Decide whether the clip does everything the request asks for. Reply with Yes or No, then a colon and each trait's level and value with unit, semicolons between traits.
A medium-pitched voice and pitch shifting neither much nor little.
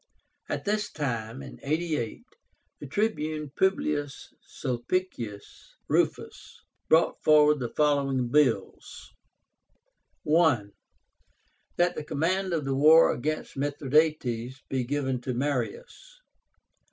Yes: medium, 145 Hz; average, 3.7 semitones